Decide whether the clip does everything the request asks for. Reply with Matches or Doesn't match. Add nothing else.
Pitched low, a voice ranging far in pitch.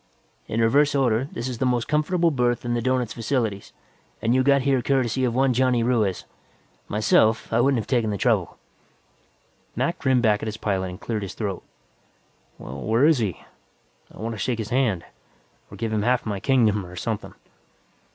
Doesn't match